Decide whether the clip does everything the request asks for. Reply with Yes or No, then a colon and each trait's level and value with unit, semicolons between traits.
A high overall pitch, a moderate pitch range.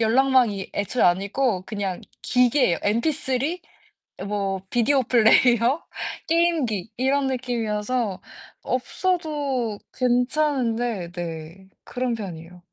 Yes: high, 240 Hz; average, 4.7 semitones